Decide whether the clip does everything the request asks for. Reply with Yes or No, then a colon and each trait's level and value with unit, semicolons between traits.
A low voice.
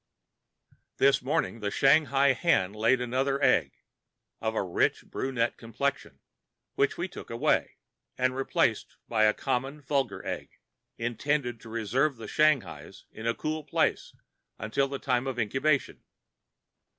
Yes: low, 130 Hz